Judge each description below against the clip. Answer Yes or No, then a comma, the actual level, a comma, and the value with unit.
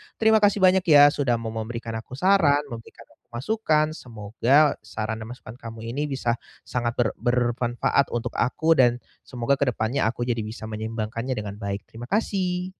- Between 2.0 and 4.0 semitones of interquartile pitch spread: No, average, 4.5 semitones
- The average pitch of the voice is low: Yes, low, 120 Hz